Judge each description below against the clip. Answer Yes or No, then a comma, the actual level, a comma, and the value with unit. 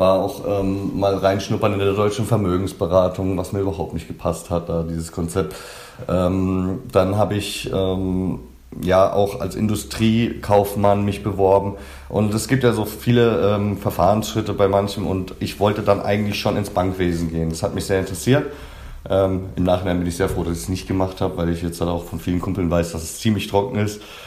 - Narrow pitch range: Yes, narrow, 2.3 semitones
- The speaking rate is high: Yes, fast, 200 wpm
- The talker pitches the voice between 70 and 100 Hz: Yes, very low, 95 Hz